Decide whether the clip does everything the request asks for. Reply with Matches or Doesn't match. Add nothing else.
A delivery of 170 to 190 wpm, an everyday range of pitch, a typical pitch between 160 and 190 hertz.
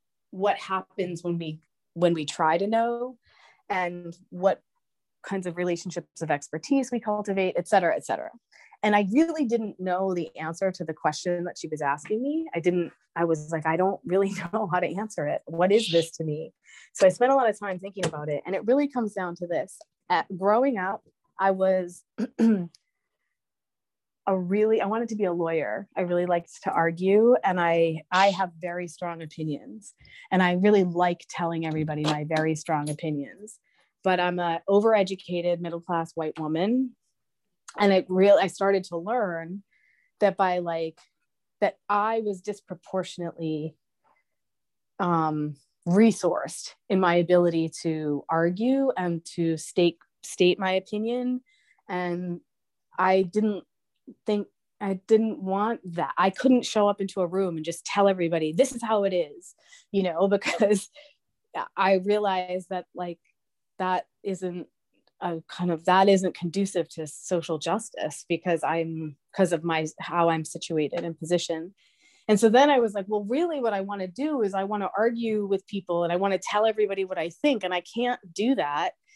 Matches